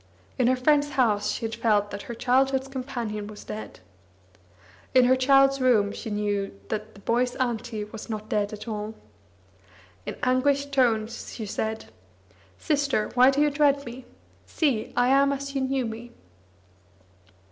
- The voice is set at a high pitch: Yes, high, 245 Hz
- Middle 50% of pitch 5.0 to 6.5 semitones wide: No, average, 4.0 semitones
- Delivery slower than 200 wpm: Yes, average, 160 wpm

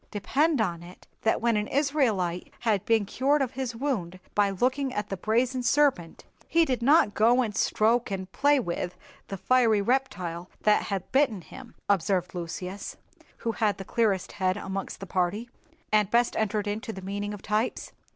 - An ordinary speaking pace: Yes, average, 175 wpm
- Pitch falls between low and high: No, high, 215 Hz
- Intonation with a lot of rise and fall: No, average, 4.7 semitones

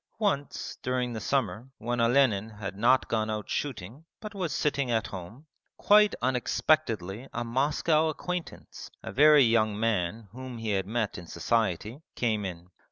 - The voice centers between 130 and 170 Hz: No, low, 120 Hz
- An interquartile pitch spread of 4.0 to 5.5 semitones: Yes, average, 4.6 semitones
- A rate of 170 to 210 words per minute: No, average, 155 wpm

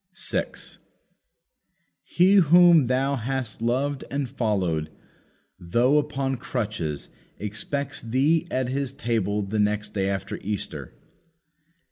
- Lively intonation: No, average, 5.0 semitones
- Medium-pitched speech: No, low, 125 Hz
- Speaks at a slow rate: Yes, slow, 105 wpm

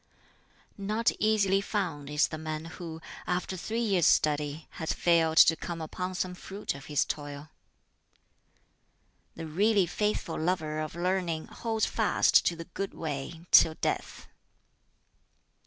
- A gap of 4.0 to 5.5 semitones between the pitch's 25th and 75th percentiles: No, average, 3.5 semitones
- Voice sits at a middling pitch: Yes, medium, 170 Hz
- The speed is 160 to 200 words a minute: No, slow, 135 wpm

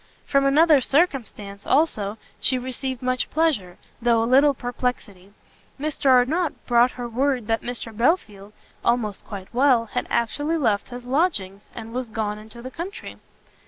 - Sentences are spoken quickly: No, average, 150 wpm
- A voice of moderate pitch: No, high, 245 Hz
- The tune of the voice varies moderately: Yes, average, 3.9 semitones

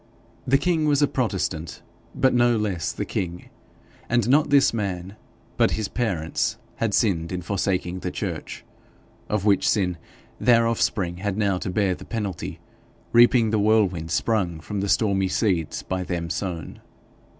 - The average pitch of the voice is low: Yes, low, 100 Hz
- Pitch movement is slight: No, average, 4.2 semitones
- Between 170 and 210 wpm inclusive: No, average, 155 wpm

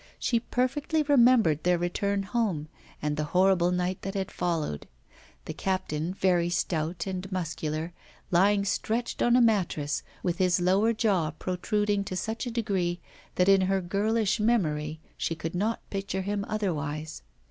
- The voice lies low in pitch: No, high, 190 Hz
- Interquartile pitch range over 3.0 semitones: Yes, average, 3.6 semitones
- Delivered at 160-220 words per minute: No, average, 150 wpm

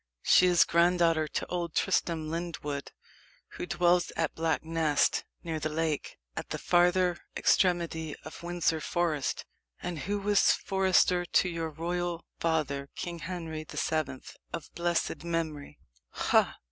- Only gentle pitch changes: Yes, narrow, 1.8 semitones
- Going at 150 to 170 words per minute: No, slow, 135 wpm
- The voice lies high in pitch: No, medium, 170 Hz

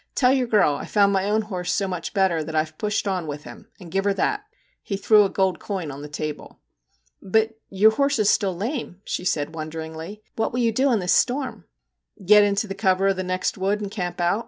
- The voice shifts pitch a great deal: No, average, 3.8 semitones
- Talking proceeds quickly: Yes, fast, 260 wpm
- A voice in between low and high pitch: No, high, 195 Hz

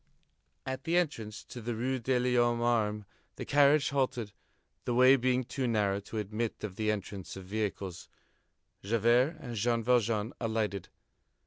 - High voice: No, low, 115 Hz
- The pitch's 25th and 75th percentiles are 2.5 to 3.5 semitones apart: Yes, average, 3.1 semitones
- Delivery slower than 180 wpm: Yes, average, 150 wpm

